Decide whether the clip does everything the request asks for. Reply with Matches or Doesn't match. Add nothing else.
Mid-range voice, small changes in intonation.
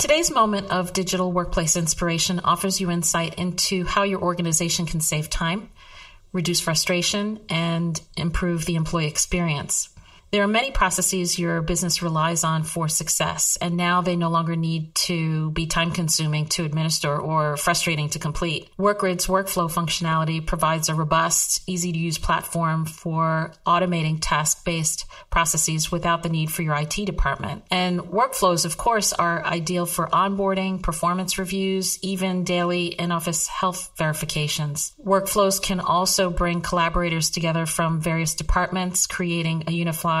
Matches